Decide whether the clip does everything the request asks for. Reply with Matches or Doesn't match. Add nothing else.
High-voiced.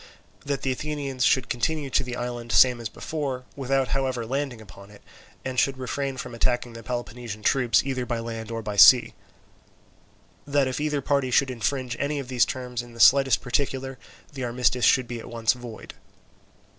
Doesn't match